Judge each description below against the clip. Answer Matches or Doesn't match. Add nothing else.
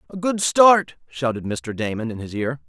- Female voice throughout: Doesn't match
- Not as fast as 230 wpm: Matches